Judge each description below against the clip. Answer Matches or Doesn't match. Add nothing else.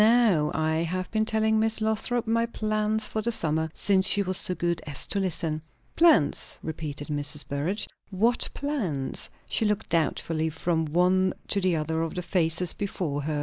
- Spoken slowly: Doesn't match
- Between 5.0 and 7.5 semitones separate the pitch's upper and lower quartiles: Matches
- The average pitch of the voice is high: Doesn't match